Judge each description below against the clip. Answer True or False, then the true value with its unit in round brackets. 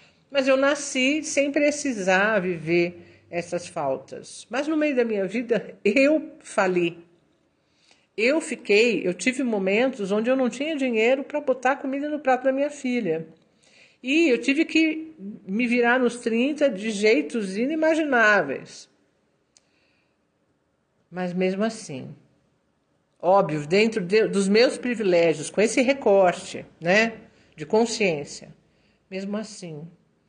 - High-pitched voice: True (225 Hz)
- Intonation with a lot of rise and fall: True (6.0 semitones)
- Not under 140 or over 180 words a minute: False (125 wpm)